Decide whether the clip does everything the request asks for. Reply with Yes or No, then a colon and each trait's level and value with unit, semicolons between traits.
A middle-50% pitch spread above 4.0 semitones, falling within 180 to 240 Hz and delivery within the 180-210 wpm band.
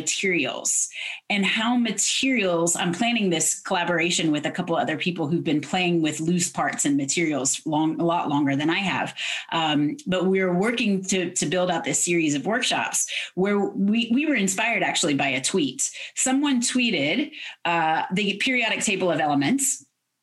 No: wide, 5.6 semitones; medium, 185 Hz; average, 170 wpm